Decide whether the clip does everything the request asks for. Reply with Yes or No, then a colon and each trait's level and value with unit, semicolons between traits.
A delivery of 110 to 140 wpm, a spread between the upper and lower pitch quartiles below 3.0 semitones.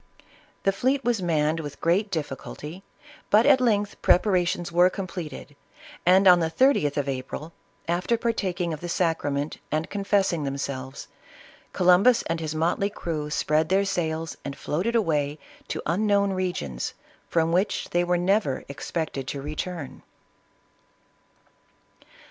No: slow, 135 wpm; average, 4.4 semitones